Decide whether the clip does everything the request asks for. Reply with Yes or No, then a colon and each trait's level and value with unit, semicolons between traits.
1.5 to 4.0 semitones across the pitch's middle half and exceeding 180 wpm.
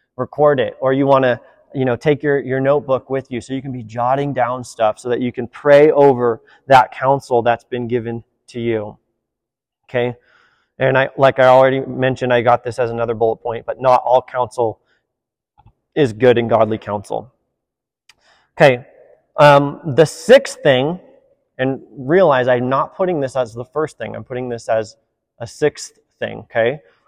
No: average, 2.8 semitones; average, 175 wpm